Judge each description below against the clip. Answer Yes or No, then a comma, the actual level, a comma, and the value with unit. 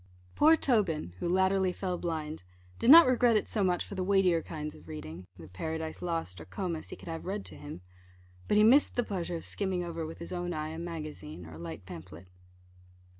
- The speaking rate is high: Yes, fast, 215 wpm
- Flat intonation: No, average, 4.0 semitones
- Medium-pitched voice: Yes, medium, 170 Hz